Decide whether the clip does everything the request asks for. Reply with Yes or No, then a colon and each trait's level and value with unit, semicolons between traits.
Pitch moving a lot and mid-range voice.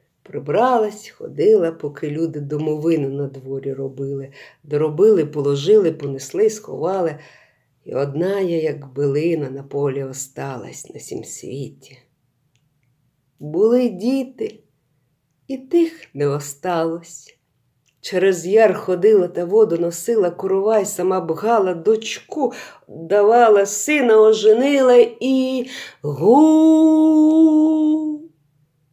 Yes: wide, 8.2 semitones; medium, 180 Hz